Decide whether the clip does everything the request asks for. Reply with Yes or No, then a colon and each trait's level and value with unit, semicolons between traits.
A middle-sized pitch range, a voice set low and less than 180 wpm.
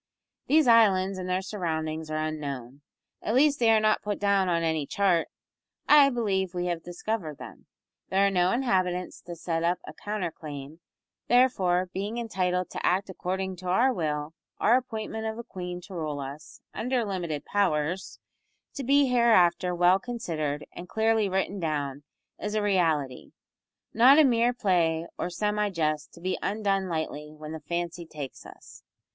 No: average, 4.9 semitones; medium, 185 Hz; average, 165 wpm